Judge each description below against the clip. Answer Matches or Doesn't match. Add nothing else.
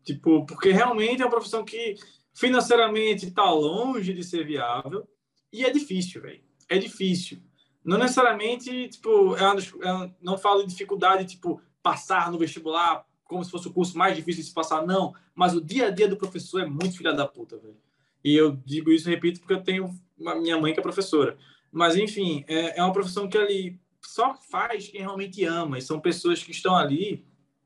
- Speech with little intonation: Doesn't match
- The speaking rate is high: Matches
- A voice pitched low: Doesn't match